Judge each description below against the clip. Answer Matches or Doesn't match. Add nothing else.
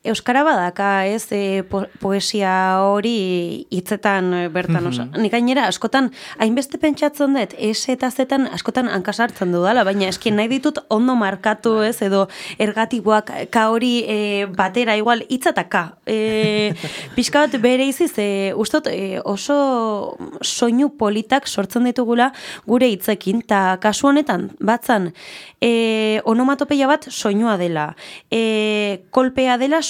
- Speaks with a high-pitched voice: Matches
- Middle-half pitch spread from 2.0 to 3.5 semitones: Doesn't match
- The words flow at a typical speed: Doesn't match